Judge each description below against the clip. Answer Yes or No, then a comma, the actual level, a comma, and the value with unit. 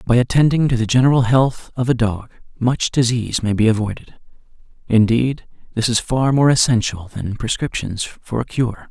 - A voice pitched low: Yes, low, 120 Hz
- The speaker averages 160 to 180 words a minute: Yes, average, 170 wpm